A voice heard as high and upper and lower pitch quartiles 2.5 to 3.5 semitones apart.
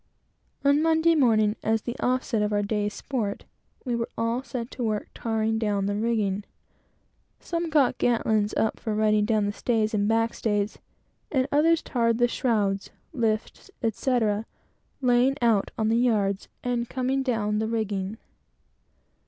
Yes: high, 225 Hz; average, 2.8 semitones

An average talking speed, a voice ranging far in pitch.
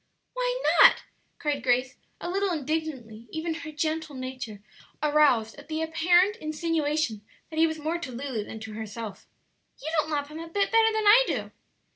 No: average, 175 wpm; average, 4.4 semitones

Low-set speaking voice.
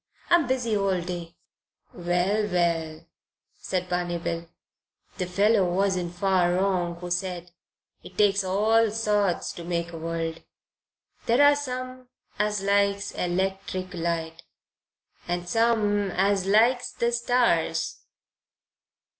No: high, 190 Hz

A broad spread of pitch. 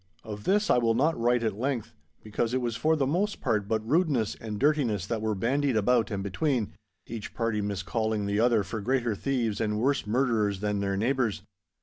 No: average, 3.7 semitones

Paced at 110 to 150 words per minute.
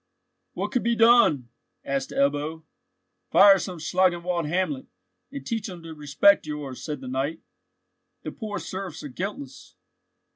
Yes: average, 140 wpm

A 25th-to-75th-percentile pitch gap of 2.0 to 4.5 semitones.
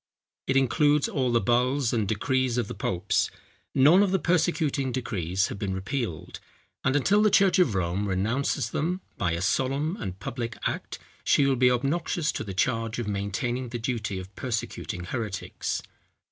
No: wide, 5.6 semitones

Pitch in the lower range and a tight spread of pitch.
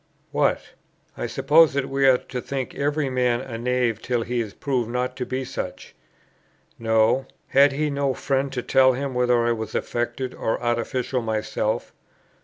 Yes: low, 125 Hz; narrow, 2.3 semitones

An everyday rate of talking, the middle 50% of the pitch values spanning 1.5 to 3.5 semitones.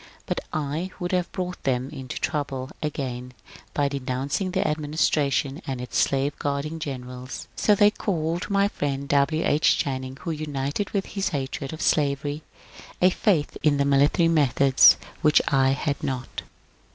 Yes: average, 150 wpm; average, 3.2 semitones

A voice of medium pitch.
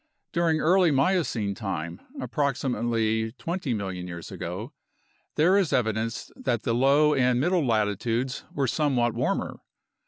No: low, 125 Hz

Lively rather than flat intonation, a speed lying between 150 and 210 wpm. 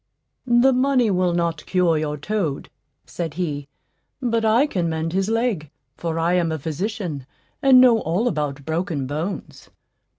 Yes: wide, 6.1 semitones; average, 155 wpm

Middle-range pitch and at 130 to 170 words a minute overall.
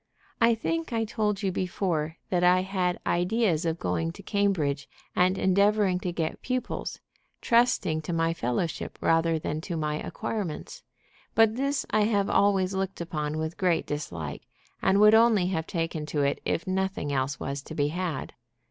Yes: medium, 180 Hz; average, 165 wpm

